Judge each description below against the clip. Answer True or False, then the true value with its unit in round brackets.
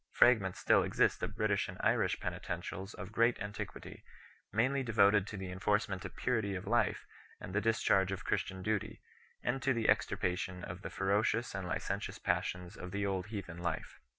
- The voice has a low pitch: True (100 Hz)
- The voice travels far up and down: False (3.0 semitones)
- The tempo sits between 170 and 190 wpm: True (175 wpm)